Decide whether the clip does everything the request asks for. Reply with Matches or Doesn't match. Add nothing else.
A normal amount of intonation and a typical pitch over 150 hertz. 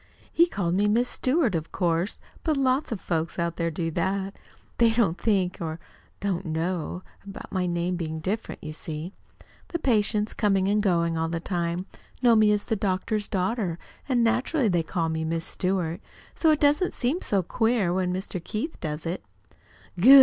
Matches